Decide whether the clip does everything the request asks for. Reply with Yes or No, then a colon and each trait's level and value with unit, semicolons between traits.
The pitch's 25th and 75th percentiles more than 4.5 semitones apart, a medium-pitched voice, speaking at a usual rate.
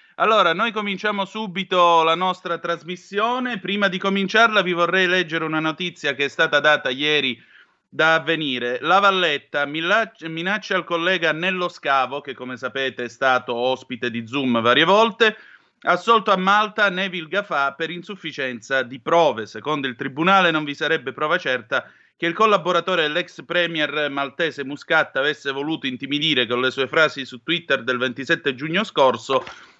Yes: average, 5.2 semitones; medium, 165 Hz; average, 155 wpm